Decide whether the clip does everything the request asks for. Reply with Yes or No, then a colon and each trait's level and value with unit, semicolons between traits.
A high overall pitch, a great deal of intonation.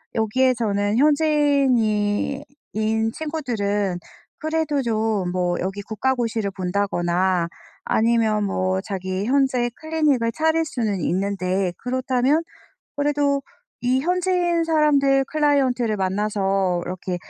Yes: high, 230 Hz; wide, 6.1 semitones